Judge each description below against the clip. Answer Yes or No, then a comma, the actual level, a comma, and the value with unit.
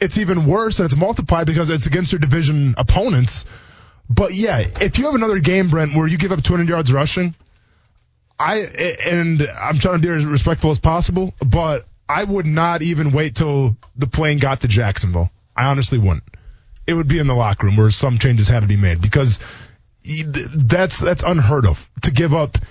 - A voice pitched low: No, medium, 145 Hz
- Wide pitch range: Yes, wide, 6.1 semitones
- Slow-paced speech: No, average, 195 wpm